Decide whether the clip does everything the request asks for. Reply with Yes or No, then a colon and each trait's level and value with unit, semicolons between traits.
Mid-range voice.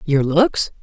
Yes: medium, 170 Hz